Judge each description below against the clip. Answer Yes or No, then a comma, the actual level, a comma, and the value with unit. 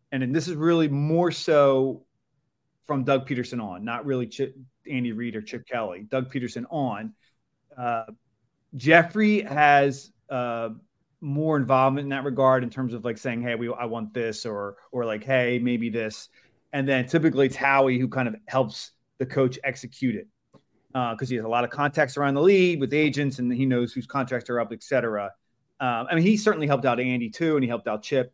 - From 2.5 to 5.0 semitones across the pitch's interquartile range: Yes, average, 2.8 semitones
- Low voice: Yes, low, 130 Hz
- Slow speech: No, fast, 205 wpm